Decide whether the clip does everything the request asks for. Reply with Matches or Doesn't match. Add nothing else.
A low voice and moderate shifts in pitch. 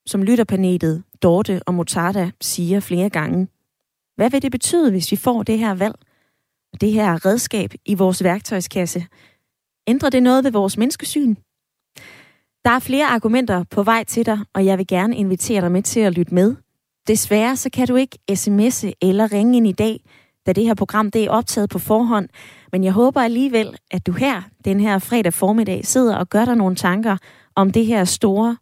Doesn't match